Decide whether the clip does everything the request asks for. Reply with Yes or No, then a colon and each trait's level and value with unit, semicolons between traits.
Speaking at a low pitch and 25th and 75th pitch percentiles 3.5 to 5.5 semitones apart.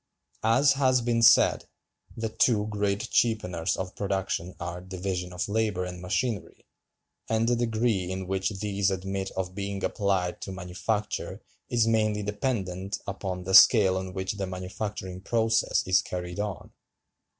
No: low, 100 Hz; average, 2.8 semitones